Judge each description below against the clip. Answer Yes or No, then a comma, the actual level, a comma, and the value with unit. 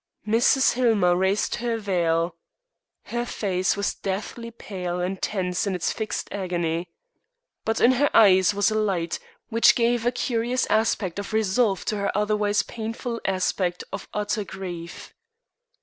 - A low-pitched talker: No, high, 205 Hz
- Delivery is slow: No, average, 145 wpm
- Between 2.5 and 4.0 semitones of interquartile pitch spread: Yes, average, 3.7 semitones